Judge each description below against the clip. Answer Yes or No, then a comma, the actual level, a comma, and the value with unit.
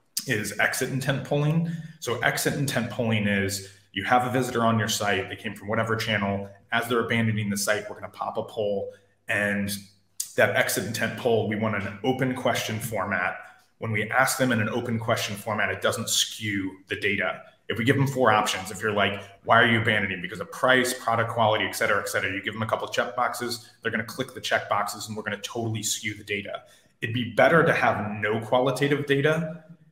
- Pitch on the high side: No, low, 115 Hz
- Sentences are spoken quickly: Yes, fast, 215 wpm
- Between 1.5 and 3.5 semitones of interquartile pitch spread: No, average, 3.9 semitones